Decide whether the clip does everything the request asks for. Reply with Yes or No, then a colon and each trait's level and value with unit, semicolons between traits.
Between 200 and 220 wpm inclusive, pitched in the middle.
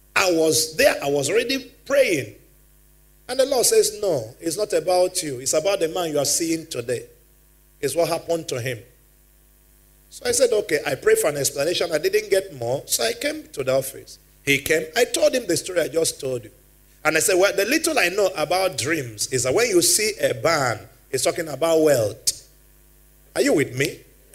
Yes: fast, 205 wpm; medium, 170 Hz